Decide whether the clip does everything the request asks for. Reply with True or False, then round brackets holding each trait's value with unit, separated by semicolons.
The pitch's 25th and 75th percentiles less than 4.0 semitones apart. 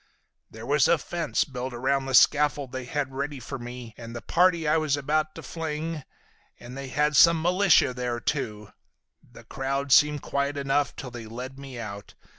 True (3.1 semitones)